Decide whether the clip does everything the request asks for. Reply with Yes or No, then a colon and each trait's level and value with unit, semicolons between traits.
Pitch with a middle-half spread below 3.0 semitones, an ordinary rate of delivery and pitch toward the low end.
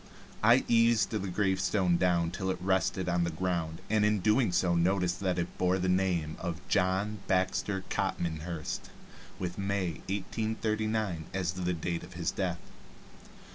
Yes: narrow, 2.5 semitones; average, 150 wpm; very low, 95 Hz